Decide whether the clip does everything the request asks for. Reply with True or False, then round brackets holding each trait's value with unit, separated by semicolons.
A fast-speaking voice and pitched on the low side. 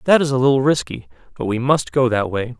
True (255 wpm; 125 Hz)